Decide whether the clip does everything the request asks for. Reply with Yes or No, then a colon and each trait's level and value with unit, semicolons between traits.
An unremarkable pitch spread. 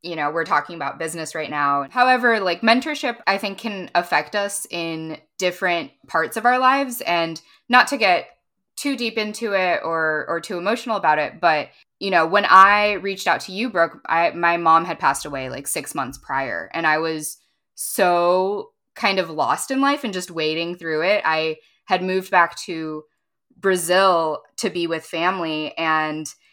Yes: average, 4.4 semitones